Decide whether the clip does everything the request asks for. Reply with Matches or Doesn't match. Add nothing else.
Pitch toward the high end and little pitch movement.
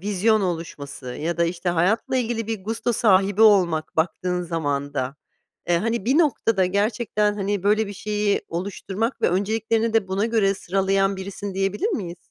Doesn't match